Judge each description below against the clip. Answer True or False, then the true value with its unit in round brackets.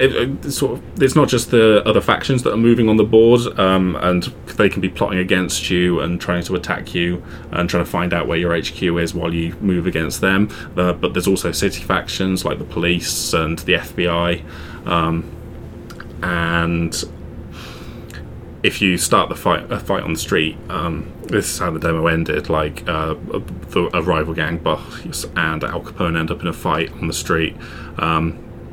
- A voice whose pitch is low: True (85 Hz)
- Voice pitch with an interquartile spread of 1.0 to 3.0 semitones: True (2.4 semitones)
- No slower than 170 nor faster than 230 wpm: True (190 wpm)